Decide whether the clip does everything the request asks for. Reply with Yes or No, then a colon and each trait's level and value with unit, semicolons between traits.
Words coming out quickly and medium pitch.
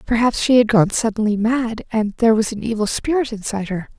No: fast, 210 wpm; high, 225 Hz